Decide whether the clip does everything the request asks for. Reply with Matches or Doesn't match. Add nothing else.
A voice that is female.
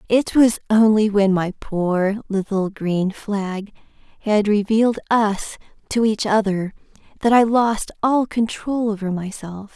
Matches